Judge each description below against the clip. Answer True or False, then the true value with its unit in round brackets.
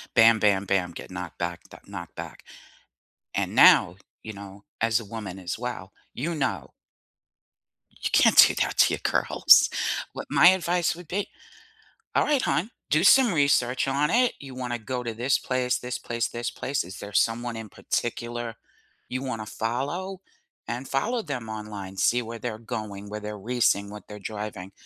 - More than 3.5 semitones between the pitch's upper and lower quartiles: True (4.5 semitones)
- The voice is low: True (115 Hz)